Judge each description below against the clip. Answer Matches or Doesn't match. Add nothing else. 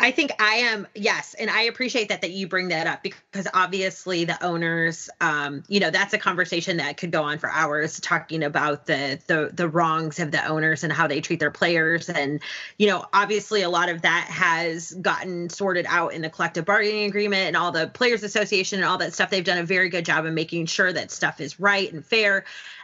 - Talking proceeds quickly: Matches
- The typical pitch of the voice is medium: Matches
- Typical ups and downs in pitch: Matches